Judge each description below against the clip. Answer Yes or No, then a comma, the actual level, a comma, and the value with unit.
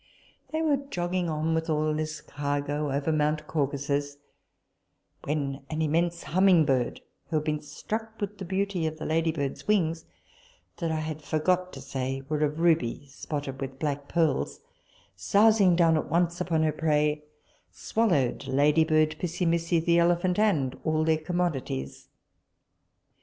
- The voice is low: No, medium, 155 Hz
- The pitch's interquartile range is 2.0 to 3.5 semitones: Yes, average, 3.0 semitones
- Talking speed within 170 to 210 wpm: No, average, 145 wpm